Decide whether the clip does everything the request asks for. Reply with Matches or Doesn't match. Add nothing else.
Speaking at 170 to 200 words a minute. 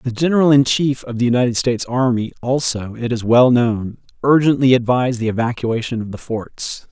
Matches